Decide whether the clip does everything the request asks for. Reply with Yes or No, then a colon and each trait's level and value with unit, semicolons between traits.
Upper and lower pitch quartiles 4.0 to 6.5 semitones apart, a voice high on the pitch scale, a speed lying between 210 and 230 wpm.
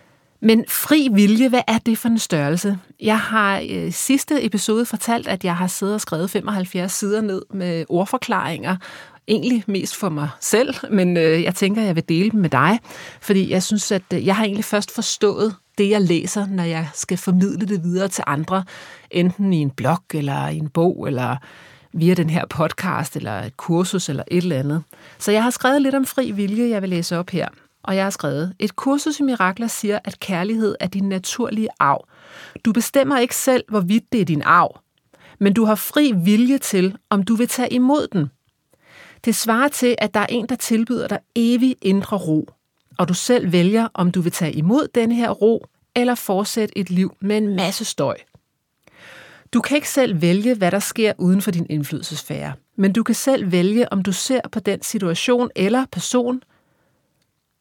No: average, 4.5 semitones; high, 200 Hz; average, 195 wpm